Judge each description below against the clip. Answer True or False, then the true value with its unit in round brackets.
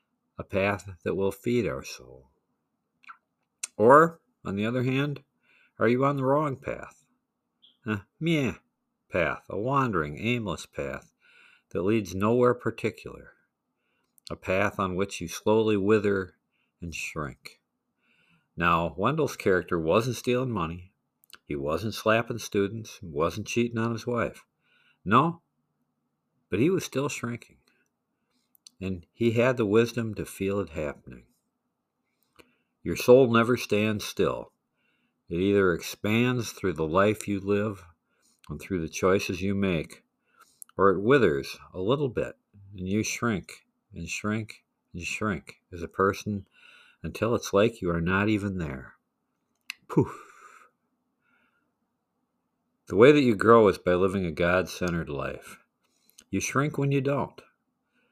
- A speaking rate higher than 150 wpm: False (135 wpm)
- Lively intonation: False (4.5 semitones)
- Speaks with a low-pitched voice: True (105 Hz)